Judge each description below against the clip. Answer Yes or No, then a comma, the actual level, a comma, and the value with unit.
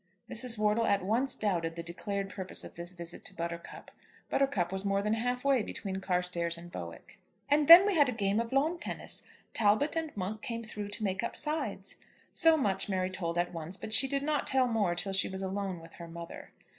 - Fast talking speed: Yes, fast, 215 wpm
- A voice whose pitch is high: Yes, high, 200 Hz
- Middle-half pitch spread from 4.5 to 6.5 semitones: Yes, wide, 5.6 semitones